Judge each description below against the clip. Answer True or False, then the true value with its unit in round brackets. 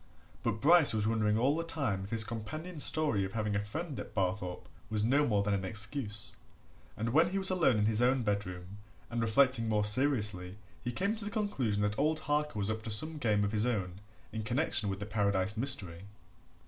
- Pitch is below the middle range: True (110 Hz)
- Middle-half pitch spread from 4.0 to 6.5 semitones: True (5.5 semitones)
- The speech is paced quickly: True (210 wpm)